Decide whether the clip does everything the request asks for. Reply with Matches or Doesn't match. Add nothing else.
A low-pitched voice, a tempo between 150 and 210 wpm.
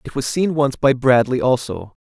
Matches